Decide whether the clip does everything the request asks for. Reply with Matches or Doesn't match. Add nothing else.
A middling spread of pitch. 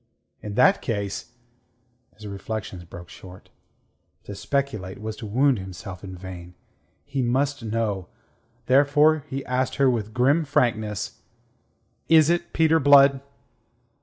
Doesn't match